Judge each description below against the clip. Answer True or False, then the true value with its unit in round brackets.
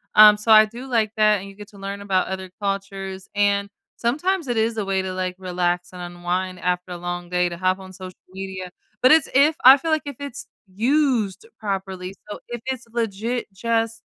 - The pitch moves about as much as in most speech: True (3.8 semitones)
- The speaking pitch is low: False (200 Hz)